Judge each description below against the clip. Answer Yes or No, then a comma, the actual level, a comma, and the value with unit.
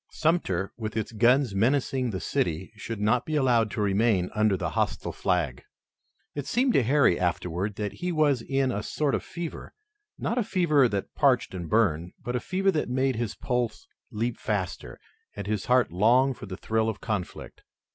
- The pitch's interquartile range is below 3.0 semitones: No, average, 5.1 semitones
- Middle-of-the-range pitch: No, low, 115 Hz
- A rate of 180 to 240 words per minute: Yes, average, 185 wpm